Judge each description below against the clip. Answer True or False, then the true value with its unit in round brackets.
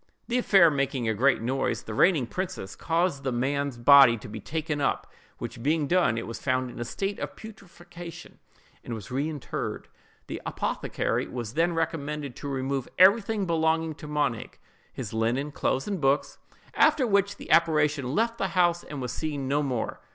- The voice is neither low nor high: True (145 Hz)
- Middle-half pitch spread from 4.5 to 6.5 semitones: True (5.0 semitones)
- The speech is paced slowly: False (170 wpm)